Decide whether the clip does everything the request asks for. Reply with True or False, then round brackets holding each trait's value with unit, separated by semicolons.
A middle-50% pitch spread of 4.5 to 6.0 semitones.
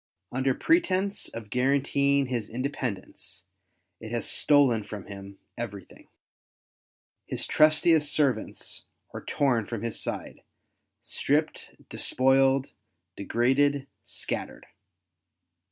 False (3.8 semitones)